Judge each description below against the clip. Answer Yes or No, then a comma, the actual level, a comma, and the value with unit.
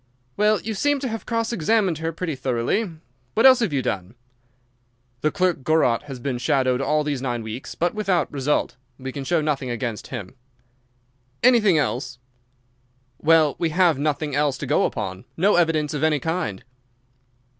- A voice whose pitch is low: No, medium, 150 Hz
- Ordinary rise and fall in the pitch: No, wide, 5.7 semitones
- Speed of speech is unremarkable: Yes, average, 165 wpm